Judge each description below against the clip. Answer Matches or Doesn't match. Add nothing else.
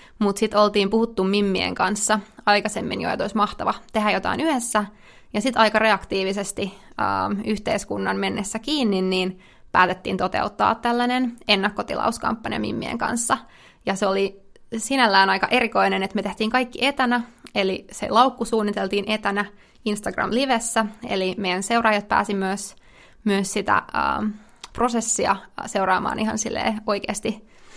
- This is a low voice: Doesn't match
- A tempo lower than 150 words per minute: Matches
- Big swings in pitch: Doesn't match